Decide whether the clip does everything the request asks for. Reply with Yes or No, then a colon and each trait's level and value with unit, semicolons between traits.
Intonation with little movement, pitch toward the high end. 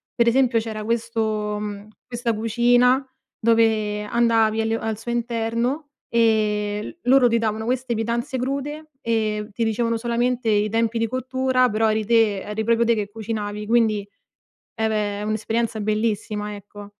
Yes: narrow, 1.9 semitones; high, 225 Hz